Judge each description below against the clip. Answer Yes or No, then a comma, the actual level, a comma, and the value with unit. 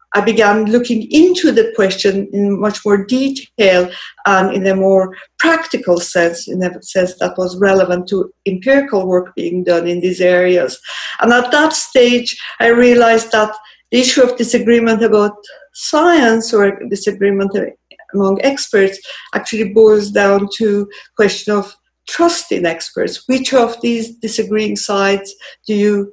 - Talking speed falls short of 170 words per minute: Yes, average, 150 wpm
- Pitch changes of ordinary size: Yes, average, 3.5 semitones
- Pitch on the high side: Yes, high, 210 Hz